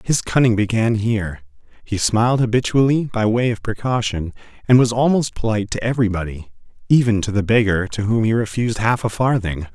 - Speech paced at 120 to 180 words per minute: Yes, average, 170 wpm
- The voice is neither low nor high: No, low, 110 Hz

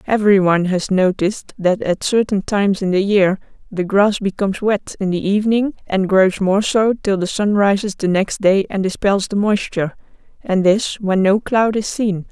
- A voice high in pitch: Yes, high, 200 Hz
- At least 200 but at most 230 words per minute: No, average, 190 wpm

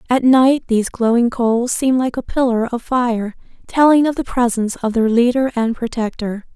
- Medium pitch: No, high, 240 Hz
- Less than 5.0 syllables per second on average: No, 5.1 syllables/s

